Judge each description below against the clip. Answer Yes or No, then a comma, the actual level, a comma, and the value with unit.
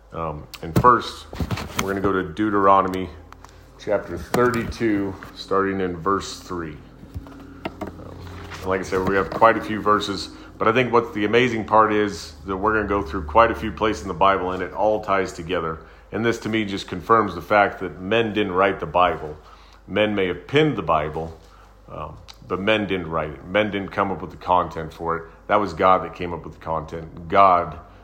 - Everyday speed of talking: No, fast, 210 wpm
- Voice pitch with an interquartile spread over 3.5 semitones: No, average, 3.2 semitones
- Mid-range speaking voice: No, very low, 95 Hz